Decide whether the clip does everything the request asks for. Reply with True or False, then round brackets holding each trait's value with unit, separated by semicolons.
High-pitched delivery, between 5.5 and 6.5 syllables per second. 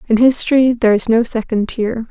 True (230 Hz; 5.6 syllables/s)